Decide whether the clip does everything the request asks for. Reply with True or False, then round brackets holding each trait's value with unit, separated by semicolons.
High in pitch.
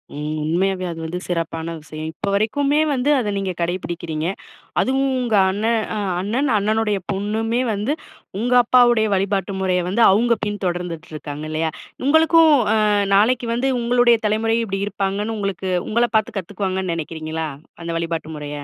True (200 Hz)